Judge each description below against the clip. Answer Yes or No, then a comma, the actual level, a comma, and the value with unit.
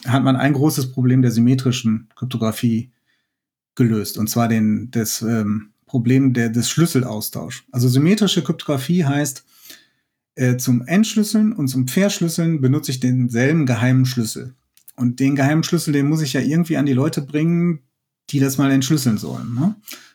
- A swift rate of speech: No, average, 150 wpm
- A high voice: No, low, 135 Hz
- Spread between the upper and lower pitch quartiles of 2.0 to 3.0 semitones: No, average, 3.8 semitones